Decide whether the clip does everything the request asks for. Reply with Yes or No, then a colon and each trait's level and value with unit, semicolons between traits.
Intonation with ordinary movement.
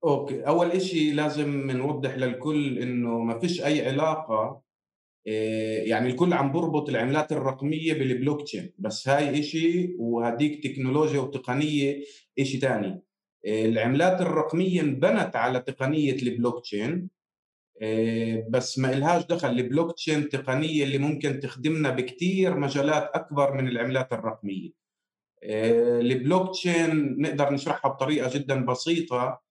Yes: average, 3.6 semitones